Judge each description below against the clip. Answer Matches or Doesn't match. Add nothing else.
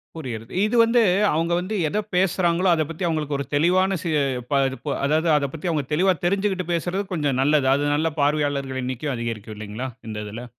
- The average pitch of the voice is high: Doesn't match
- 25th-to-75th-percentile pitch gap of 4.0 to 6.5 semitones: Matches